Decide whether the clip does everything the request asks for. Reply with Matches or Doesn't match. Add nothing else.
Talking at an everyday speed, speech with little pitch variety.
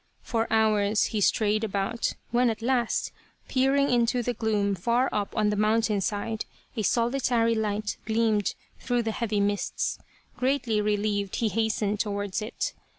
Matches